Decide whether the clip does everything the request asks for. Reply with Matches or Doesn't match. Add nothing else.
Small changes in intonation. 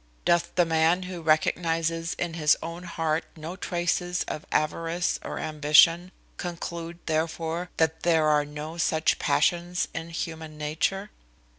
Matches